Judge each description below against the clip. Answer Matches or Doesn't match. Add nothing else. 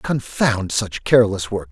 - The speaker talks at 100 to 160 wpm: Matches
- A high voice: Doesn't match